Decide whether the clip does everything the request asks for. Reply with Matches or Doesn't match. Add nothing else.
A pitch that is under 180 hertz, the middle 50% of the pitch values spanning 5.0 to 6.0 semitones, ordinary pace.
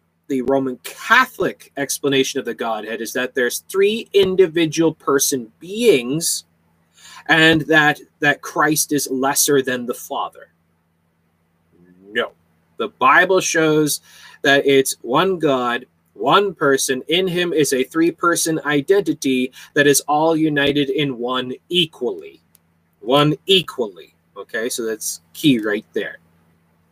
Doesn't match